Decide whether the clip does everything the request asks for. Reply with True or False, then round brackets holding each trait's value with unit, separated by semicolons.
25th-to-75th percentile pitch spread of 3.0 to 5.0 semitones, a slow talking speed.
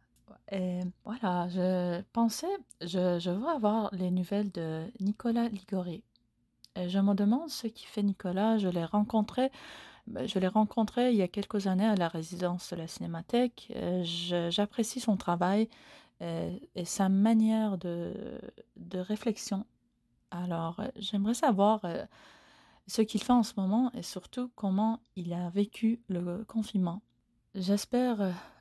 True (3.8 semitones; 140 wpm)